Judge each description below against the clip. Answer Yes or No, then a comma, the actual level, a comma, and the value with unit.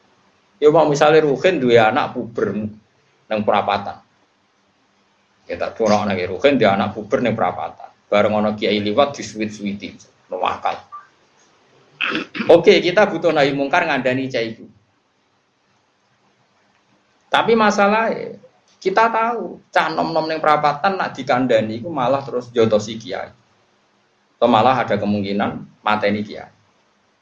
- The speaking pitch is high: No, low, 130 Hz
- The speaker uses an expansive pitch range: Yes, wide, 7.7 semitones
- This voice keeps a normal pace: Yes, average, 125 wpm